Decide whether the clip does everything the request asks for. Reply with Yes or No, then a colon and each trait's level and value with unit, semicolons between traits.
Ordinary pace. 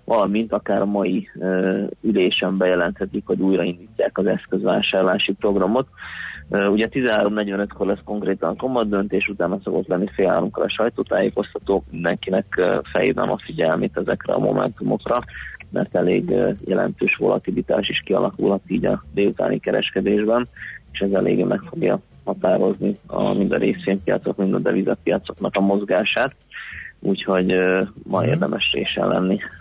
Yes: average, 135 wpm